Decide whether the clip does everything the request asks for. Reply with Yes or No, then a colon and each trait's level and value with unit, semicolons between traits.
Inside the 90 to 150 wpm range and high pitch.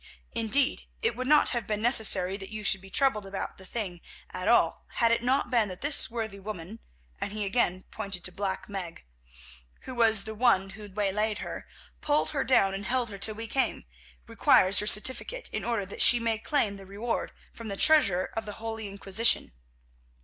No: average, 195 wpm; high, 215 Hz